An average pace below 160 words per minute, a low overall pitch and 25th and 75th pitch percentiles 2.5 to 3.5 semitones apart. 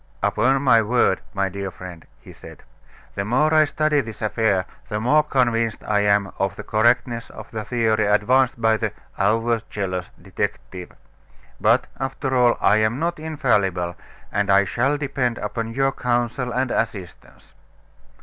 No: average, 150 wpm; low, 115 Hz; average, 4.0 semitones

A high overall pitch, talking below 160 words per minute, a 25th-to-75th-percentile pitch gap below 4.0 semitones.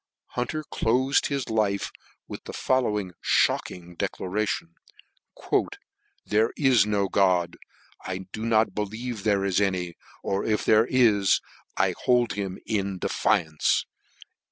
No: low, 105 Hz; slow, 135 wpm; average, 3.3 semitones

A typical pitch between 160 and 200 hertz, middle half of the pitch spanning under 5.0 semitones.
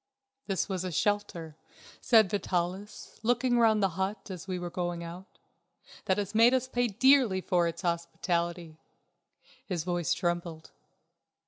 Yes: medium, 185 Hz; average, 3.4 semitones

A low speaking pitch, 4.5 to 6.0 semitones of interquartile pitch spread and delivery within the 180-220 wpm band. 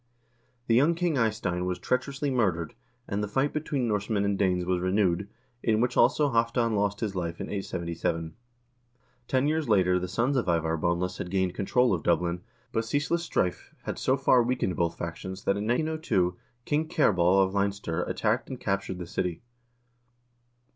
No: low, 100 Hz; wide, 5.6 semitones; average, 170 wpm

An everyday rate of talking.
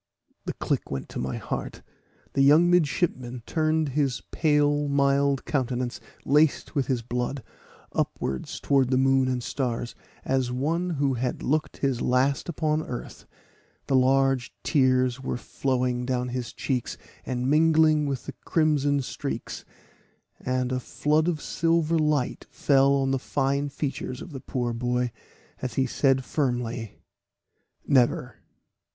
Yes: average, 145 wpm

